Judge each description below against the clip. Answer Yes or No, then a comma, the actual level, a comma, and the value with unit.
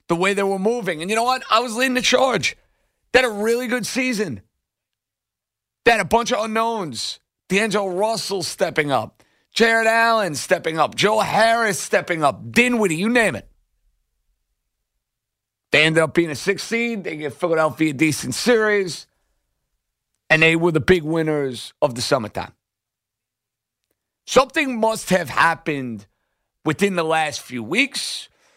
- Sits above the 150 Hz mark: Yes, medium, 185 Hz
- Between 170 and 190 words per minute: No, average, 155 wpm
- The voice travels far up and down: Yes, wide, 7.3 semitones